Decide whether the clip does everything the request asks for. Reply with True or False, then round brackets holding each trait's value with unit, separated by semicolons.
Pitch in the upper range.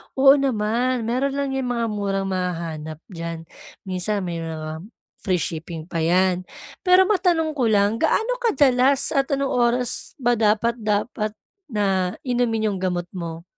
True (210 Hz)